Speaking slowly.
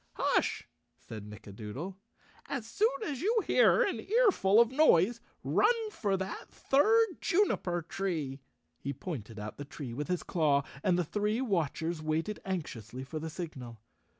No: average, 155 wpm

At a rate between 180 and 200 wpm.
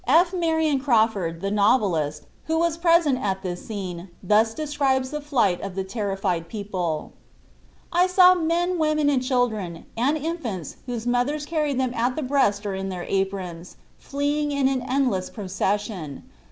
No: average, 155 wpm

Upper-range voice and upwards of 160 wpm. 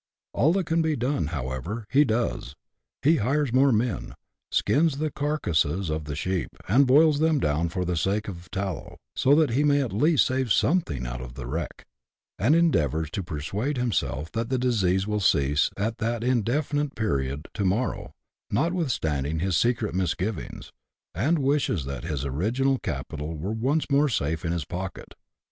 No: low, 105 Hz; average, 170 wpm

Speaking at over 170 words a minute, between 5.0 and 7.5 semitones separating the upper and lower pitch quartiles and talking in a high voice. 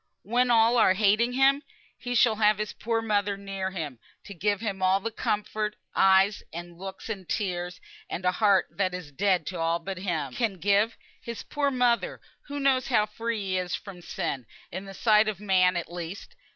No: average, 200 wpm; average, 3.4 semitones; high, 200 Hz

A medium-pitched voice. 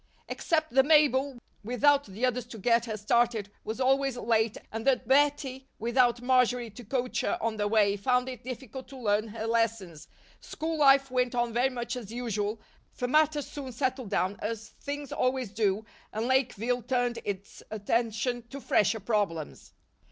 No: high, 245 Hz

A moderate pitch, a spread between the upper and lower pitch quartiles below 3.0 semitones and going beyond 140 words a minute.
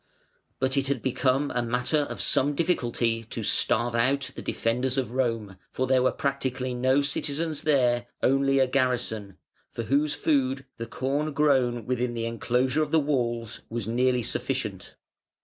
No: low, 130 Hz; narrow, 2.6 semitones; average, 160 wpm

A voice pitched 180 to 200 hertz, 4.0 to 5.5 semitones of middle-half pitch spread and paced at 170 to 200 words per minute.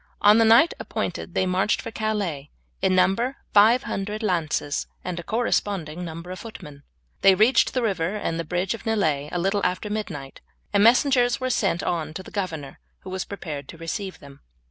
Yes: high, 190 Hz; average, 4.6 semitones; average, 185 wpm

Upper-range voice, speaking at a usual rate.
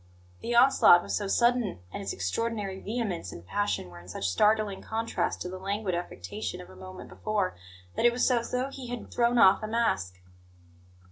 Yes: high, 205 Hz; average, 190 wpm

